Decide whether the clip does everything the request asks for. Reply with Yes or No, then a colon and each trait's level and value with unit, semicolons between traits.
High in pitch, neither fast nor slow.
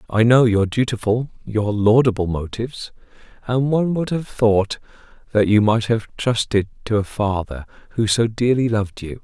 No: low, 110 Hz; average, 160 wpm